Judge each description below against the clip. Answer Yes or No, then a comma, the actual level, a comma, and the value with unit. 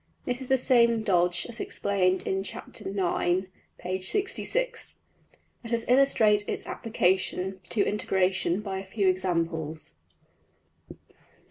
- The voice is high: Yes, high, 195 Hz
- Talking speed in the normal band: No, slow, 115 wpm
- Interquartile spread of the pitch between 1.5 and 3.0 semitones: No, average, 3.9 semitones